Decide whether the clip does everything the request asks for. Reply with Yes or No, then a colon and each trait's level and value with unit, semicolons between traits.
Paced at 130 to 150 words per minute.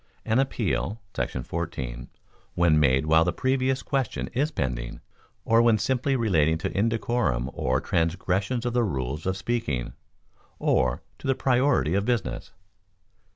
Yes: average, 140 wpm